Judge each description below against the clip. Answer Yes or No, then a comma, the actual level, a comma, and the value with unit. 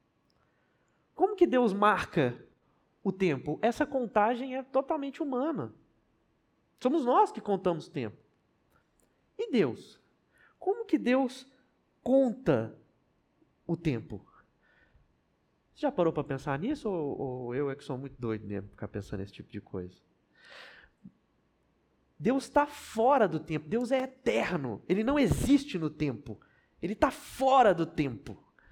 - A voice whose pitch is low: No, high, 195 Hz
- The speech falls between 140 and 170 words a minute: No, average, 130 wpm